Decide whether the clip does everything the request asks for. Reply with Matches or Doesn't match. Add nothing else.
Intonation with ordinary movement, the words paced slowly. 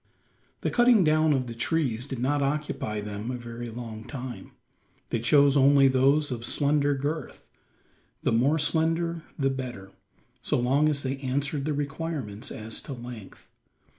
Doesn't match